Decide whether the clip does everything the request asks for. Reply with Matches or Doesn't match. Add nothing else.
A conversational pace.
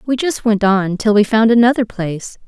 Doesn't match